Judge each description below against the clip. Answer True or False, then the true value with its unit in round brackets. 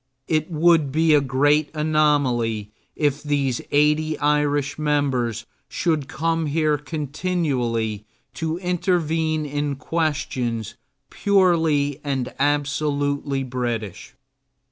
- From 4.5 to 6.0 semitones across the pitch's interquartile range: False (2.8 semitones)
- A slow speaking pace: True (95 wpm)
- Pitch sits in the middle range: True (145 Hz)